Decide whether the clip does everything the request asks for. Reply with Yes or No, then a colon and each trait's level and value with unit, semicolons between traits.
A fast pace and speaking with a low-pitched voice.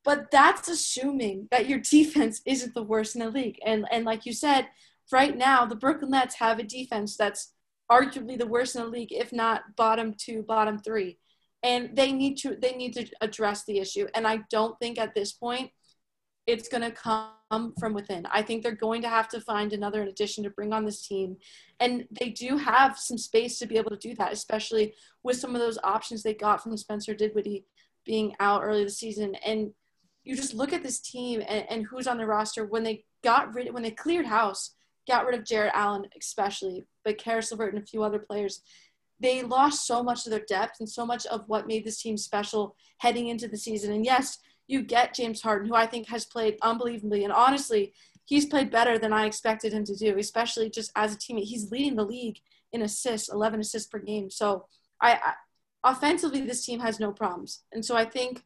No: fast, 215 wpm; high, 225 Hz